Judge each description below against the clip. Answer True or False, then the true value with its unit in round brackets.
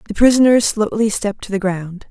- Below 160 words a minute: False (200 wpm)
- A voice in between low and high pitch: False (210 Hz)